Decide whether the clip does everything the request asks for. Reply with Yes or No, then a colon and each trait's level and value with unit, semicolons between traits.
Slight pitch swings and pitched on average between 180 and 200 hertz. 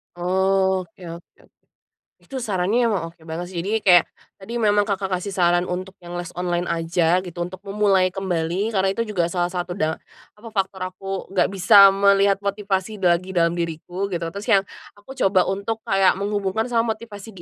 Yes: narrow, 2.3 semitones; high, 190 Hz